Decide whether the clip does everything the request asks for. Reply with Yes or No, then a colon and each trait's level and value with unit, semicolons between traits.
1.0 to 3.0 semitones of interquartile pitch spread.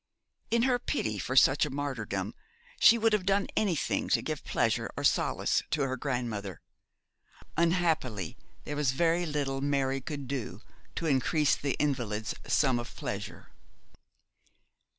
No: average, 4.7 semitones